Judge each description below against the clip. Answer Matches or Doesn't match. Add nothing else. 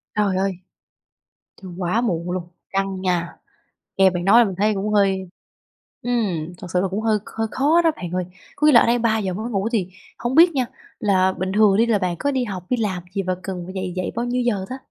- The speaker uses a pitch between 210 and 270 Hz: Doesn't match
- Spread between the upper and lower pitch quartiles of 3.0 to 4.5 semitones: Matches